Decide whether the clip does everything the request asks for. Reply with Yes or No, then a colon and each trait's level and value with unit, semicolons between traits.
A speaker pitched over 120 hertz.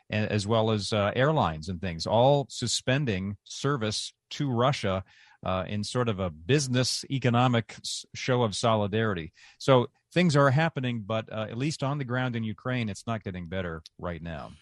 No: low, 115 Hz